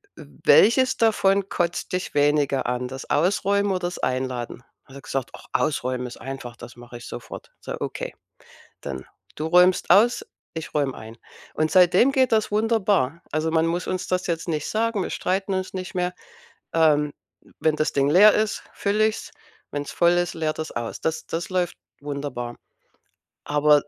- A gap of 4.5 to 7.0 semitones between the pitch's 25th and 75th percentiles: Yes, average, 5.3 semitones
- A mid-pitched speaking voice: Yes, medium, 165 Hz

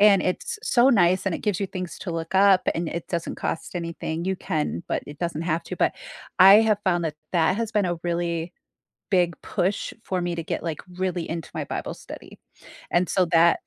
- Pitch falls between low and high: Yes, medium, 175 Hz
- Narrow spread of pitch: Yes, narrow, 2.2 semitones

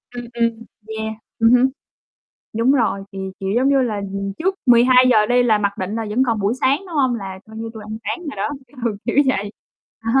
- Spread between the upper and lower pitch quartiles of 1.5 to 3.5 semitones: Yes, average, 3.1 semitones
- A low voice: No, high, 230 Hz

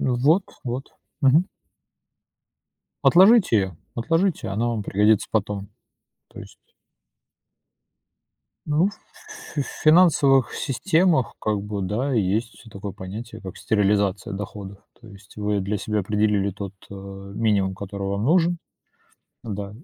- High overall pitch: No, low, 105 Hz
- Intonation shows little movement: No, average, 5.2 semitones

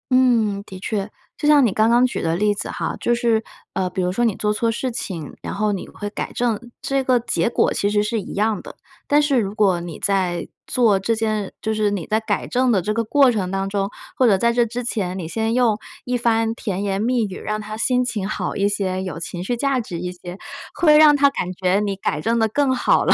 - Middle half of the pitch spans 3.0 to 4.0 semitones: Yes, average, 3.7 semitones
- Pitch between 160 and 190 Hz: No, high, 215 Hz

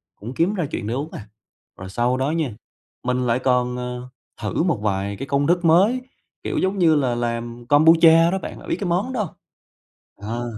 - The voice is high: No, low, 130 Hz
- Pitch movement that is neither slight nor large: No, wide, 5.8 semitones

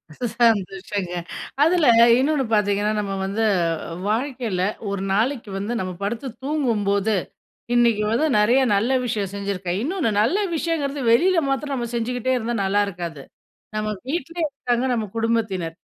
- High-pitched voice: Yes, high, 225 Hz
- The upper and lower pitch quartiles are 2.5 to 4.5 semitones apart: No, average, 5.0 semitones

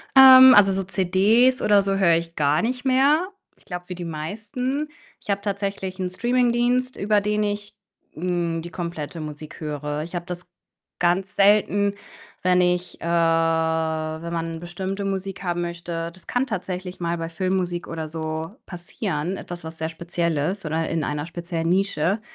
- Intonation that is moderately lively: Yes, average, 3.4 semitones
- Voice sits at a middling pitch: Yes, medium, 180 Hz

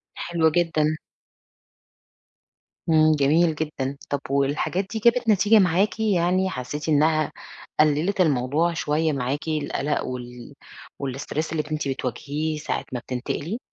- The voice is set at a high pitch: No, medium, 155 Hz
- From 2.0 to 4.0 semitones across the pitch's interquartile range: Yes, average, 3.5 semitones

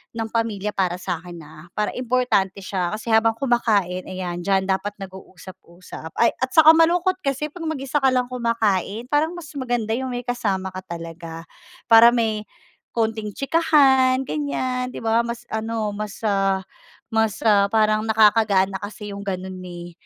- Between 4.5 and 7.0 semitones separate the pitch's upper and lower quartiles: Yes, average, 4.8 semitones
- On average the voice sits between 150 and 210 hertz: No, high, 220 Hz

